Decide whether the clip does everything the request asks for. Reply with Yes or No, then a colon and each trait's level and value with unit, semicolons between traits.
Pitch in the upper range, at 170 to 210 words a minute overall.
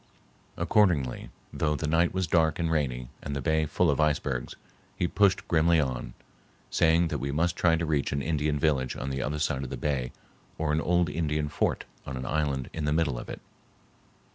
No: very low, 75 Hz; average, 200 wpm